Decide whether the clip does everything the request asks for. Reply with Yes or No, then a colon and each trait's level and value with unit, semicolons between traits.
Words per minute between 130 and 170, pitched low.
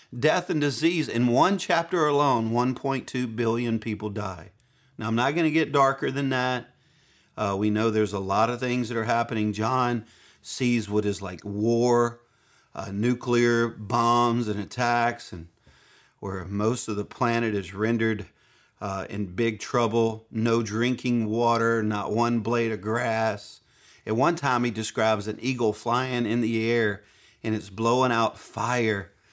Yes: average, 160 wpm; low, 115 Hz